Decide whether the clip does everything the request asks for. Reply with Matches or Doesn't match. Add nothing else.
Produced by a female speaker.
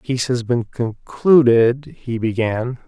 Doesn't match